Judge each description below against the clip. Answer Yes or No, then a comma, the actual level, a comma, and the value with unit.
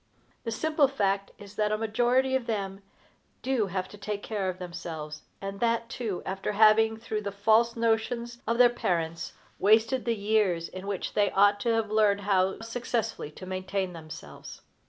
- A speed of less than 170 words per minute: No, average, 175 wpm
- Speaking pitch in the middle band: No, high, 210 Hz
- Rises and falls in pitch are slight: No, average, 3.1 semitones